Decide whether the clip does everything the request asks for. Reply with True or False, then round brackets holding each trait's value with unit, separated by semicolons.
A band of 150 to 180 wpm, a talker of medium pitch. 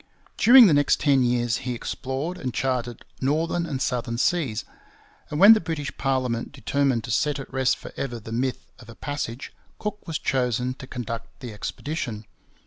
False (175 wpm; 130 Hz)